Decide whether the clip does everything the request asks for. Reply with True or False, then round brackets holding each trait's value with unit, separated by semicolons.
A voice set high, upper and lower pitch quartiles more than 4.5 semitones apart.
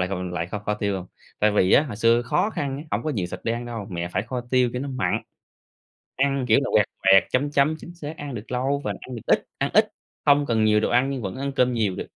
False (120 Hz; 4.9 semitones)